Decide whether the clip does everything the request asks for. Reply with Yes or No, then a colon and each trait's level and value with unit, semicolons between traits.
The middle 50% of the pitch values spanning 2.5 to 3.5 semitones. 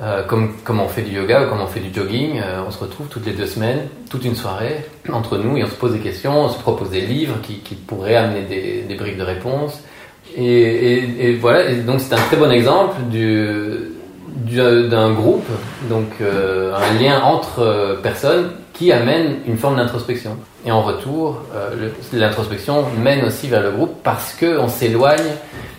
No: average, 4.3 semitones